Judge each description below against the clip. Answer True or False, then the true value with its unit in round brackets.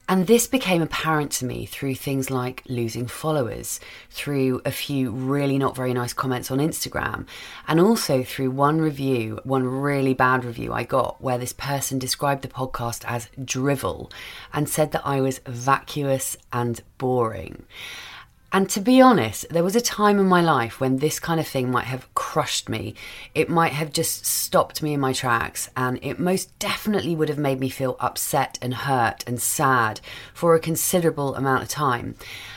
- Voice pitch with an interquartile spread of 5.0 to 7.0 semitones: False (3.8 semitones)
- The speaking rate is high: False (180 wpm)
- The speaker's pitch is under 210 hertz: True (135 Hz)